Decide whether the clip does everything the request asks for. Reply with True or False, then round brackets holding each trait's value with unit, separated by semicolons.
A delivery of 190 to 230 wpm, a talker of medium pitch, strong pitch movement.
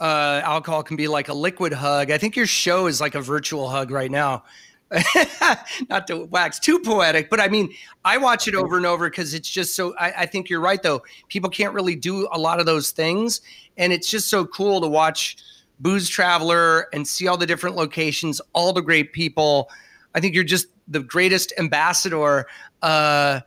False (200 wpm; 170 Hz; 3.3 semitones)